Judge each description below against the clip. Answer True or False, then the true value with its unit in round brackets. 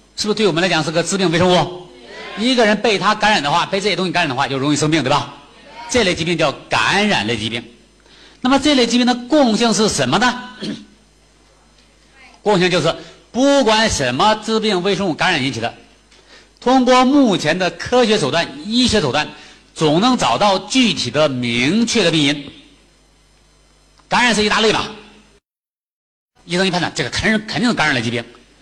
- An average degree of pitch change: False (7.2 semitones)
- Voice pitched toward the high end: True (195 Hz)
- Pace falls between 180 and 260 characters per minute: False (275 characters per minute)